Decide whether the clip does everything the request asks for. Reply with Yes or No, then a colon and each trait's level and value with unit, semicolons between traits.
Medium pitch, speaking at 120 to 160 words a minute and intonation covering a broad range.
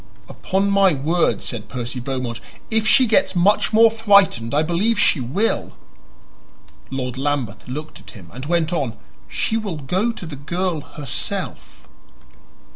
Yes: medium, 160 Hz; average, 150 wpm; wide, 7.3 semitones